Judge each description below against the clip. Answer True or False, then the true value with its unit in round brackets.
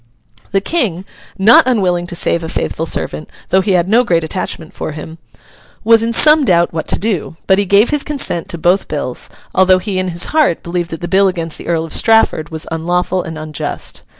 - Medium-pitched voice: True (180 Hz)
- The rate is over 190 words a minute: True (205 wpm)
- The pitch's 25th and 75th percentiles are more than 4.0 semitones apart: False (3.6 semitones)